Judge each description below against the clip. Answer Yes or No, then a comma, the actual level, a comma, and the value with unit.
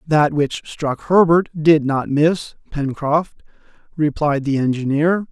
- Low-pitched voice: No, medium, 150 Hz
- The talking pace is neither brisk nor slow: No, slow, 125 wpm